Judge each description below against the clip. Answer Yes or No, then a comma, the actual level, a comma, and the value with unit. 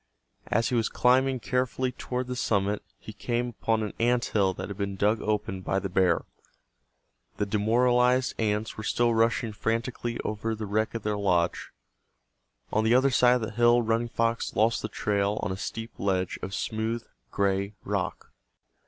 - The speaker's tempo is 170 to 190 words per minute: Yes, average, 175 wpm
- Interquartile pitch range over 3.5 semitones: No, average, 2.7 semitones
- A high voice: No, low, 110 Hz